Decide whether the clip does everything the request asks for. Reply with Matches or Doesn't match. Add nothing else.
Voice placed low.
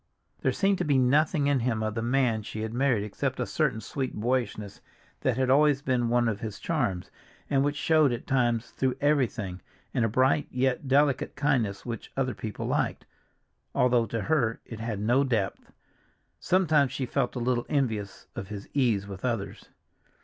Matches